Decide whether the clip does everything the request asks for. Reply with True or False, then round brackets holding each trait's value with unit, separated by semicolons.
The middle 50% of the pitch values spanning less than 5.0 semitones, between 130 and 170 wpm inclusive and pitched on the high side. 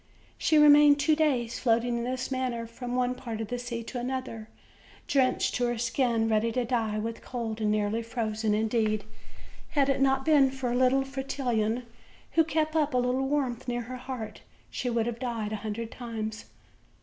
False (2.8 semitones; 185 wpm; 245 Hz)